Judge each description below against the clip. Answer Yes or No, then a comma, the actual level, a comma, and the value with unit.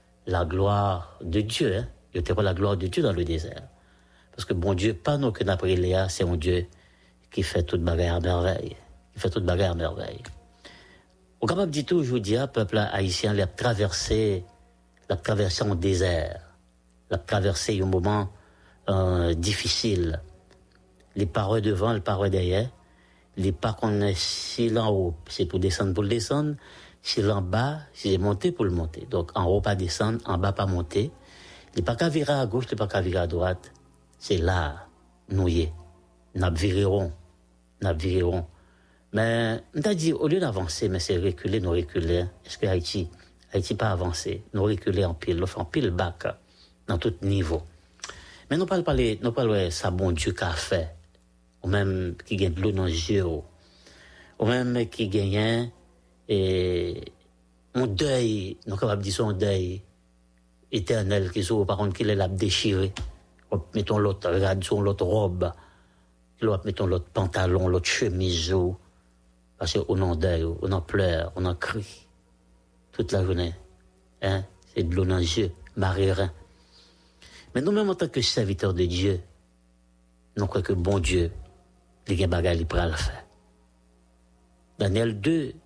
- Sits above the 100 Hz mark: No, very low, 95 Hz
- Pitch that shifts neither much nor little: Yes, average, 3.5 semitones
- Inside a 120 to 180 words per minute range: Yes, average, 160 wpm